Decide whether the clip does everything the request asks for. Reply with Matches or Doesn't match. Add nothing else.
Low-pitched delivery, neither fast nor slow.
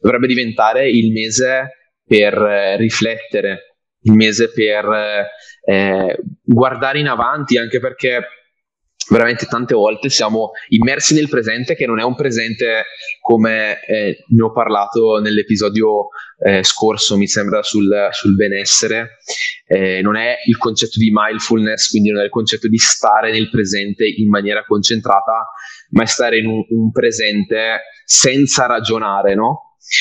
Matches